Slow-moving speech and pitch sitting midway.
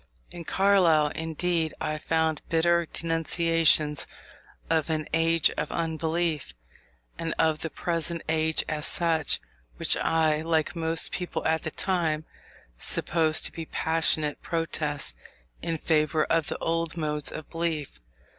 Yes: slow, 130 wpm; medium, 160 Hz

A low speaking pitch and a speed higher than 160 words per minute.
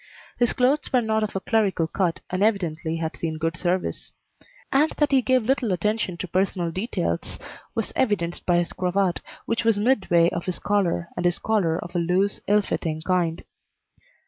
No: medium, 185 Hz; average, 180 wpm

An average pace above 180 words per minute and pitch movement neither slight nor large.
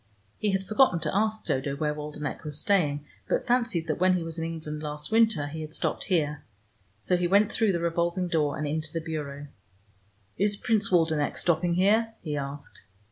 Yes: average, 190 wpm; average, 4.6 semitones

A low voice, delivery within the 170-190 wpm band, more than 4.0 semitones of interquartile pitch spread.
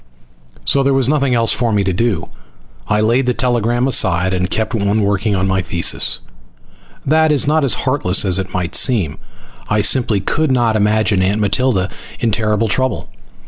Yes: low, 110 Hz; average, 180 wpm; average, 4.6 semitones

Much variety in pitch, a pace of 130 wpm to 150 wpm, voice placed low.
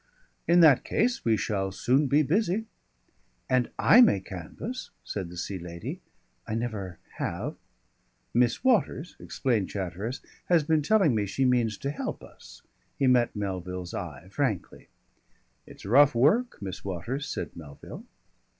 Yes: wide, 7.7 semitones; average, 145 wpm; low, 120 Hz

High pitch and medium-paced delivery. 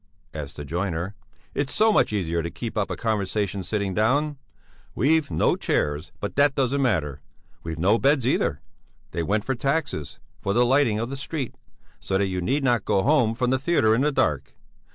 No: low, 110 Hz; average, 195 wpm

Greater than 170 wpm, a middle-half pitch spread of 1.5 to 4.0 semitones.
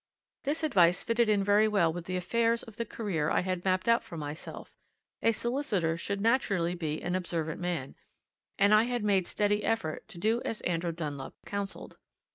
No: average, 185 wpm; average, 4.8 semitones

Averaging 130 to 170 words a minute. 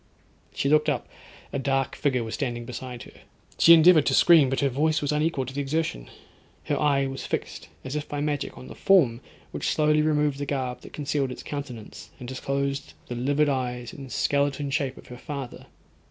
No: average, 195 wpm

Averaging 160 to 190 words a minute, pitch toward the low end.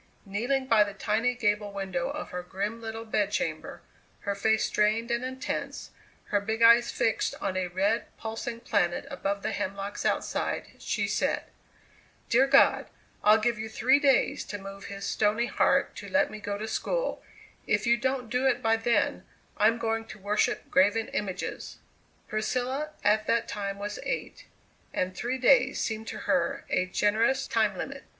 No: average, 165 wpm; high, 220 Hz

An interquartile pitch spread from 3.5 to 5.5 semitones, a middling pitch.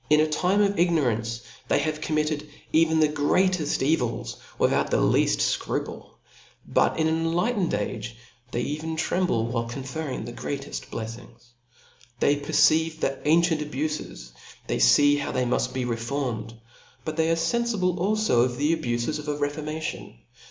Yes: average, 4.7 semitones; medium, 150 Hz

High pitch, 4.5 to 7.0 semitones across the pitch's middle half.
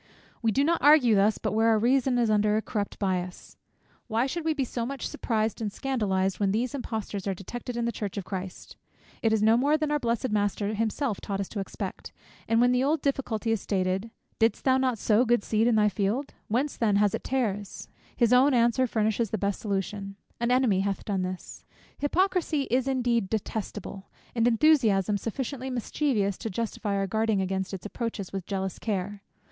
No: high, 220 Hz; average, 3.8 semitones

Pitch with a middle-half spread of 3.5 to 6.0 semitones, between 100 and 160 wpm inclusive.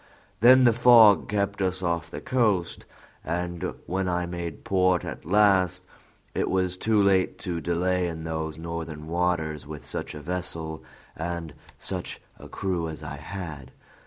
No: narrow, 2.6 semitones; average, 155 wpm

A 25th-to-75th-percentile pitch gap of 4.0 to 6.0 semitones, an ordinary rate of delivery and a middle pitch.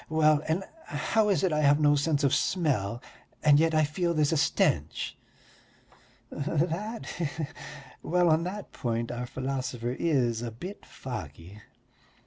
Yes: average, 4.9 semitones; average, 150 wpm; medium, 150 Hz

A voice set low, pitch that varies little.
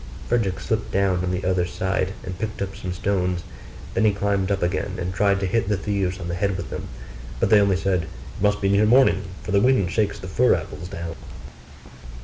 Yes: very low, 95 Hz; narrow, 2.0 semitones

